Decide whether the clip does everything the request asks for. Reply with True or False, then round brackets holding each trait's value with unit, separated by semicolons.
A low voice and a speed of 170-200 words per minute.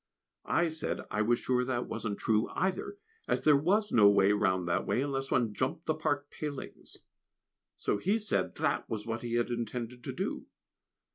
True (125 Hz; 185 wpm)